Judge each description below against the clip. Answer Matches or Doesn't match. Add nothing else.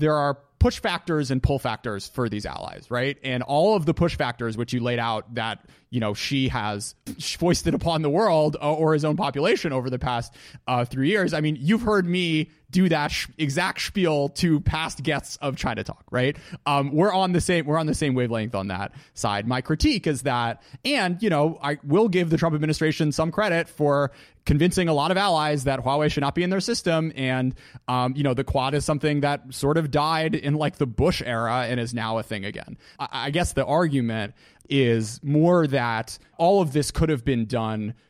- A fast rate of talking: Matches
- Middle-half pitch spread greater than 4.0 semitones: Matches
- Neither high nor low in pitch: Matches